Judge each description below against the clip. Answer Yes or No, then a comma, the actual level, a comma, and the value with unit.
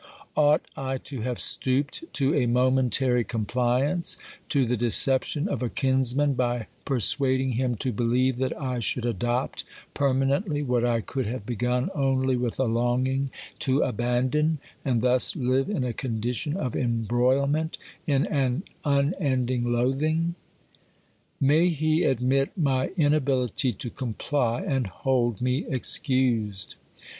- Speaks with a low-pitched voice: Yes, low, 130 Hz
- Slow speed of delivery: Yes, slow, 130 wpm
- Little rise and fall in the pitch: Yes, narrow, 2.3 semitones